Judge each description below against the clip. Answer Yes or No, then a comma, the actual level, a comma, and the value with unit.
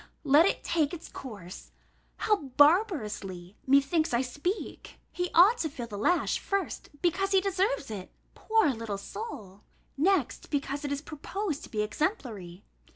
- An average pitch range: No, wide, 8.0 semitones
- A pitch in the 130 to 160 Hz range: No, very high, 290 Hz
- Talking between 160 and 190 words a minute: No, average, 150 wpm